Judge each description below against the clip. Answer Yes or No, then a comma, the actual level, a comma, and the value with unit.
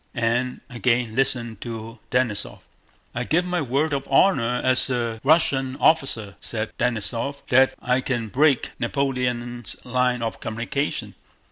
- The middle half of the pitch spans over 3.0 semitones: No, narrow, 2.5 semitones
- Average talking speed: No, slow, 130 wpm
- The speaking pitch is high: No, low, 125 Hz